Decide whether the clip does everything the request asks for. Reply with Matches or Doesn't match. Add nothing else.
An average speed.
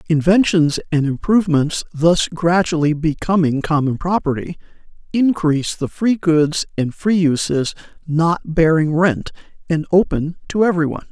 Doesn't match